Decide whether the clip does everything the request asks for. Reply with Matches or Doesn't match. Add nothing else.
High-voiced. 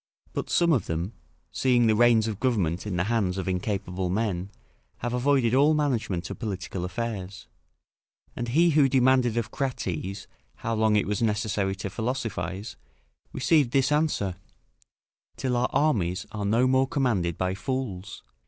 Doesn't match